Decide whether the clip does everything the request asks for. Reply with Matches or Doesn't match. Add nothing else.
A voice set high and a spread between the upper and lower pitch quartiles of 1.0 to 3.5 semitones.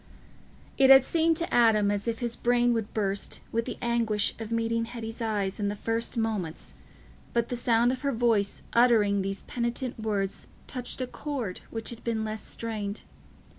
Matches